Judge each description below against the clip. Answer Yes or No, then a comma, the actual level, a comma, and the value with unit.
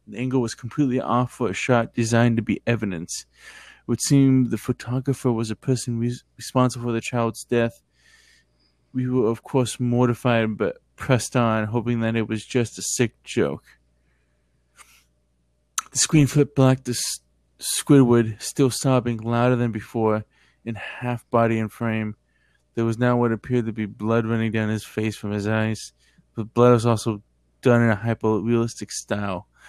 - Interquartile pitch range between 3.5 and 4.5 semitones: No, narrow, 2.4 semitones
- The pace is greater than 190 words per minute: No, average, 165 wpm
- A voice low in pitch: Yes, low, 115 Hz